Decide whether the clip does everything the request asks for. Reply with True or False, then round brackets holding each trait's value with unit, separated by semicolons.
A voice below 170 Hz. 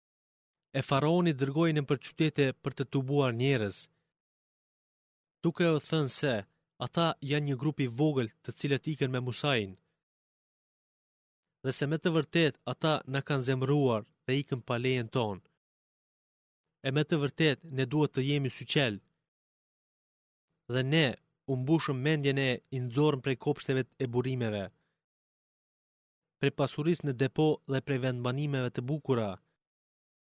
True (140 Hz)